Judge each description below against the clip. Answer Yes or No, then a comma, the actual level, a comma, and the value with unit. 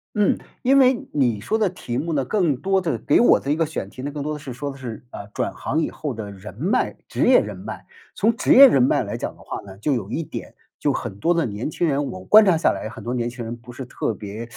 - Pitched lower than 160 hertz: Yes, medium, 140 Hz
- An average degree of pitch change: No, wide, 6.4 semitones